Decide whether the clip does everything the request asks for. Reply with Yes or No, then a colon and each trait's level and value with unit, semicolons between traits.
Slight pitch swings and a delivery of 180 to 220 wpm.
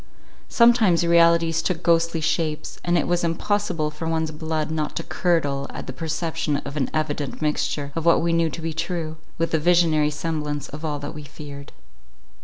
Yes: narrow, 1.8 semitones; average, 185 wpm